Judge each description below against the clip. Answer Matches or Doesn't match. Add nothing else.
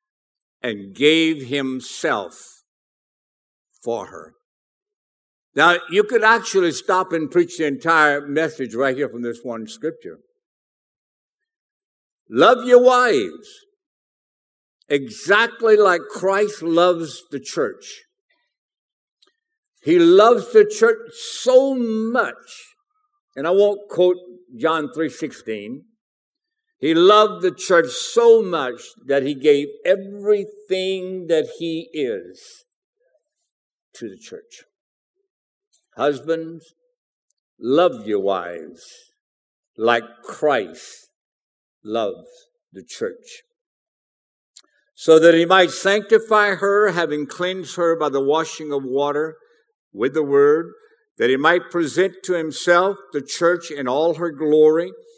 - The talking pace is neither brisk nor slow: Doesn't match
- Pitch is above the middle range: Matches